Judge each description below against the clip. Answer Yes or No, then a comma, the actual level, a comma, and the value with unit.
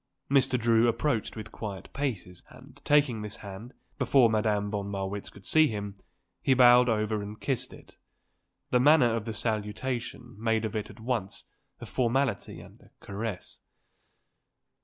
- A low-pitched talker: Yes, low, 115 Hz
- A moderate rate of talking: Yes, average, 160 wpm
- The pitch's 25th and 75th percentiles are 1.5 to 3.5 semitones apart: Yes, average, 3.2 semitones